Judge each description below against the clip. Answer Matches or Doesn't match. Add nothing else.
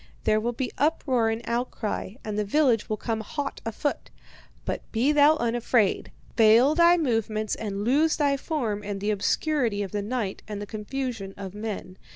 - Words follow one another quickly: Doesn't match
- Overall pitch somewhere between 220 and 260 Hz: Matches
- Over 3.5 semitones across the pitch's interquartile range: Matches